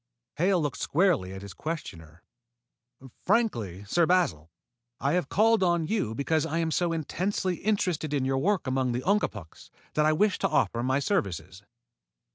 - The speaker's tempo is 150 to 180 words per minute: Yes, average, 160 wpm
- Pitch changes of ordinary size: No, wide, 7.6 semitones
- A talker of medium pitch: Yes, medium, 155 Hz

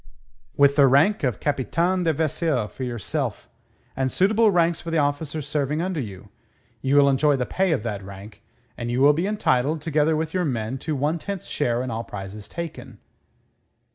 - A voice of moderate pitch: Yes, medium, 145 Hz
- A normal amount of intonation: Yes, average, 4.7 semitones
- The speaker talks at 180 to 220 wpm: Yes, average, 185 wpm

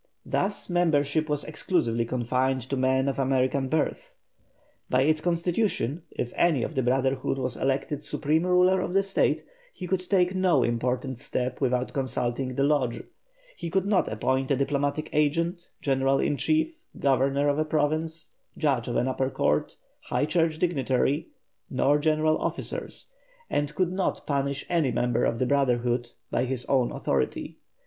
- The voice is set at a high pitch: No, medium, 140 Hz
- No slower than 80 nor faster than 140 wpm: No, average, 155 wpm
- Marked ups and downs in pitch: No, average, 3.9 semitones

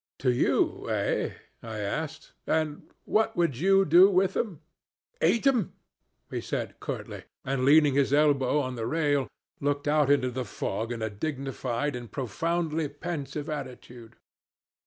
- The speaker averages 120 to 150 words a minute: Yes, average, 140 wpm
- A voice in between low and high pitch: Yes, medium, 145 Hz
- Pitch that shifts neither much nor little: Yes, average, 4.1 semitones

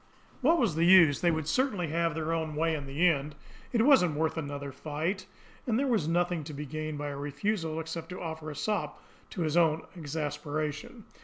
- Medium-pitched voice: Yes, medium, 160 Hz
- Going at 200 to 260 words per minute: Yes, fast, 205 wpm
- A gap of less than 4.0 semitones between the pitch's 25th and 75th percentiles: Yes, average, 3.0 semitones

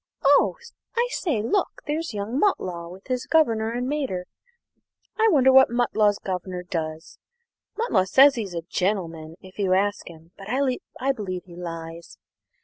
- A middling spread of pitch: No, wide, 6.8 semitones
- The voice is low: No, high, 205 Hz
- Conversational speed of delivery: Yes, average, 150 wpm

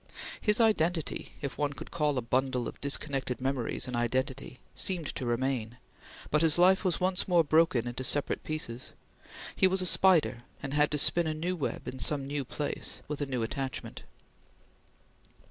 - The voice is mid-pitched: Yes, medium, 145 Hz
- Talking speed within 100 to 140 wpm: No, average, 175 wpm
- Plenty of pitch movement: No, average, 4.3 semitones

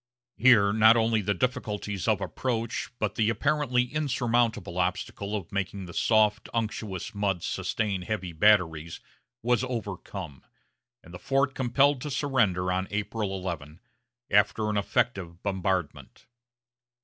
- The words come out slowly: Yes, slow, 125 wpm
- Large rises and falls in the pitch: No, average, 4.2 semitones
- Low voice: Yes, low, 105 Hz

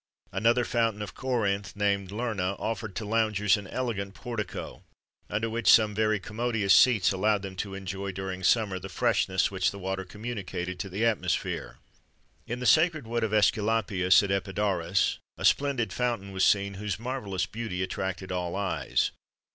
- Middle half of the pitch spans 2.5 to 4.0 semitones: Yes, average, 2.9 semitones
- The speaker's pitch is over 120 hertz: No, low, 100 Hz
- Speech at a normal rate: Yes, average, 160 wpm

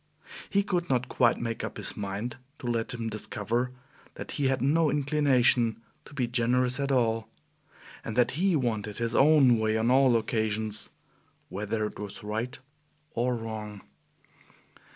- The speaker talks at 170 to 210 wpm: No, average, 150 wpm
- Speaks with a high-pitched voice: No, low, 120 Hz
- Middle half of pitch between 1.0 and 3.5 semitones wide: Yes, average, 3.2 semitones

